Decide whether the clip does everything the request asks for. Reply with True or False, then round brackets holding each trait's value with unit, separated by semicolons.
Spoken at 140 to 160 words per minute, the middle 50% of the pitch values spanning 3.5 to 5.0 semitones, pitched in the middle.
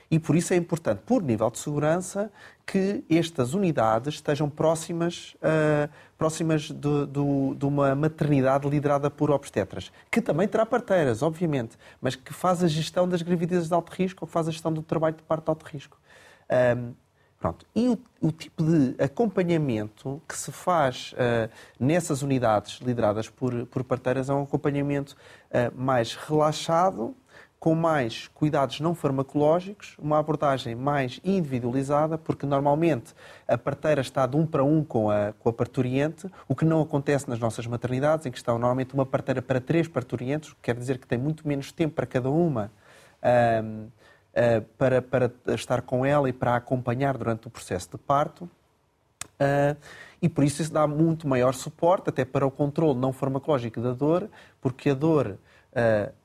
False (170 wpm; 3.9 semitones; 145 Hz)